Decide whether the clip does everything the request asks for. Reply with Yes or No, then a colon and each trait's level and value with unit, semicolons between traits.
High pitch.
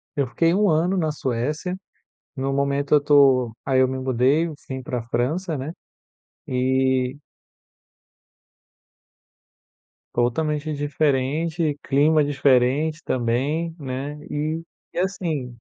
No: medium, 140 Hz